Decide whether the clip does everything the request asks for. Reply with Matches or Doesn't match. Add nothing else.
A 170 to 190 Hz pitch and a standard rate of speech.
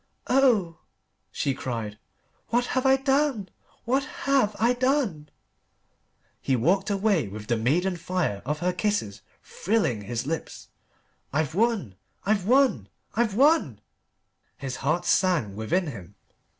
Doesn't match